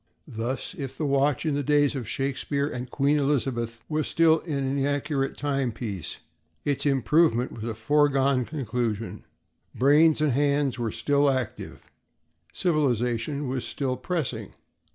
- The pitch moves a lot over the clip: No, average, 3.0 semitones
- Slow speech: Yes, slow, 130 wpm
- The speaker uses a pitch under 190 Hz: Yes, medium, 140 Hz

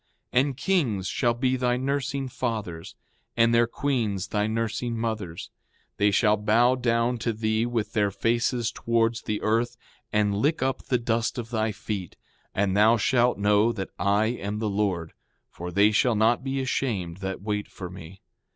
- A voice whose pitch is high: No, low, 110 Hz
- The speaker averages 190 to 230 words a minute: No, average, 170 wpm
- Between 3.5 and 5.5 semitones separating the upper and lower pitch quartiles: No, average, 2.9 semitones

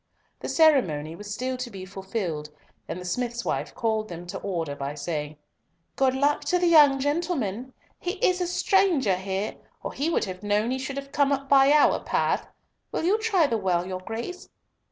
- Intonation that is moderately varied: No, wide, 7.6 semitones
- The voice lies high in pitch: Yes, high, 240 Hz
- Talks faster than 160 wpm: Yes, average, 195 wpm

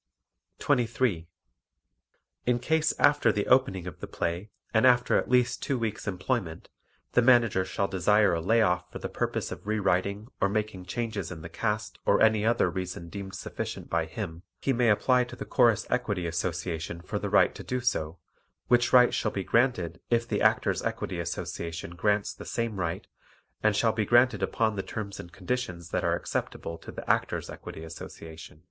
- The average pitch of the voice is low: Yes, low, 105 Hz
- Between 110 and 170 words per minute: No, average, 185 wpm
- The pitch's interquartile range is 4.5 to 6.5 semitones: Yes, average, 5.0 semitones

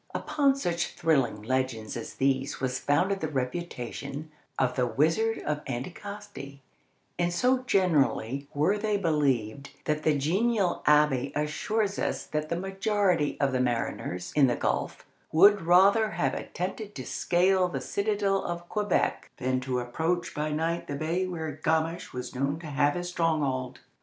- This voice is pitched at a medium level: Yes, medium, 160 Hz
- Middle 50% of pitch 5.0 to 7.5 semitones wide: Yes, wide, 5.5 semitones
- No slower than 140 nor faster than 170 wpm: Yes, average, 150 wpm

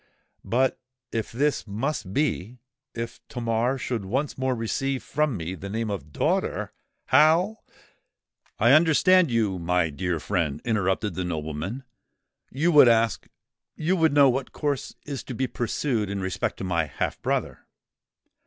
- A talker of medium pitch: No, low, 115 Hz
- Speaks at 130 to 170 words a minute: Yes, slow, 135 wpm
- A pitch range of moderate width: No, wide, 6.3 semitones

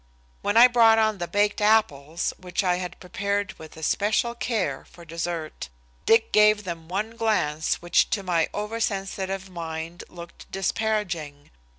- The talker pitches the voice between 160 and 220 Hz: Yes, high, 190 Hz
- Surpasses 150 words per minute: No, average, 145 wpm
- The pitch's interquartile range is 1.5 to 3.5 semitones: No, average, 4.1 semitones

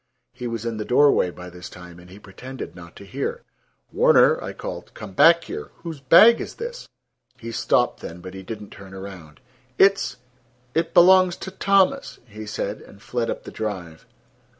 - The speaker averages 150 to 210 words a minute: Yes, average, 180 wpm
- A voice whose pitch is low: Yes, low, 115 Hz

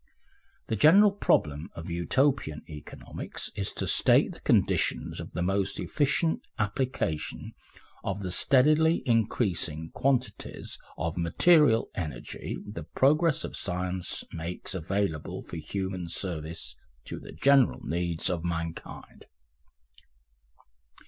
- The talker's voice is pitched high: No, very low, 95 Hz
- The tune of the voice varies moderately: No, wide, 7.8 semitones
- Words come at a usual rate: No, slow, 110 wpm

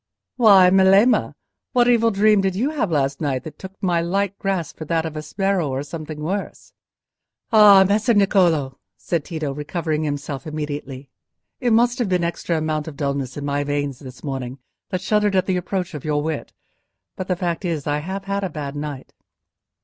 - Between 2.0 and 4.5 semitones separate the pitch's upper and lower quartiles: No, average, 5.0 semitones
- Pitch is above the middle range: No, medium, 170 Hz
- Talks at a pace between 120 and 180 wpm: No, average, 195 wpm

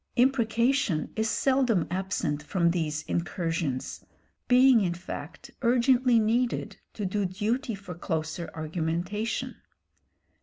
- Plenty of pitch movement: Yes, wide, 6.1 semitones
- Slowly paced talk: Yes, slow, 105 wpm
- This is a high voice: Yes, high, 200 Hz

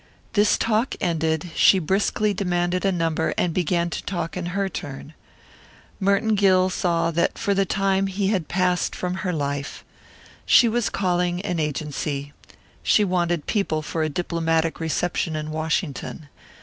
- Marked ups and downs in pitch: No, average, 3.2 semitones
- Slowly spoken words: No, average, 150 wpm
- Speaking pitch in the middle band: Yes, medium, 175 Hz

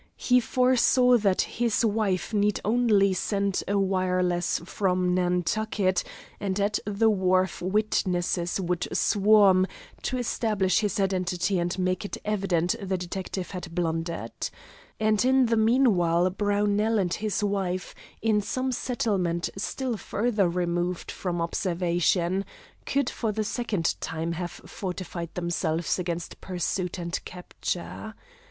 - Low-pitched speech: No, high, 190 Hz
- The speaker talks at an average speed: No, slow, 125 wpm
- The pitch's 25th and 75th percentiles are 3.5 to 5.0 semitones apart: No, average, 3.1 semitones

